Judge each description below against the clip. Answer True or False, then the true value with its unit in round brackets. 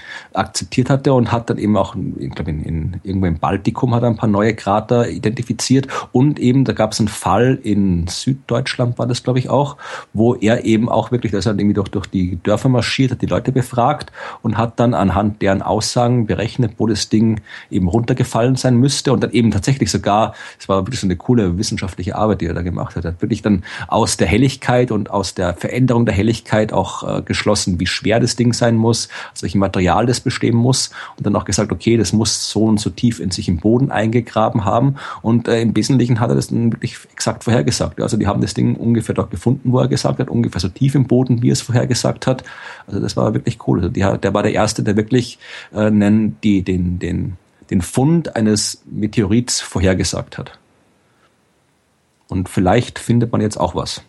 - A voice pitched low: True (110 Hz)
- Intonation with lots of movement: False (3.6 semitones)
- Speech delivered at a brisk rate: True (215 wpm)